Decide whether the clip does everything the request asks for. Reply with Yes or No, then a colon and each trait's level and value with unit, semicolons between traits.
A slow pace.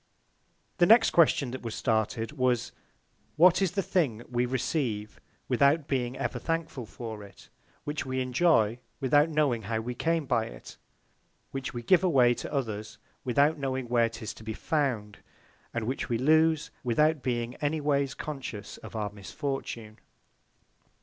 No: average, 155 wpm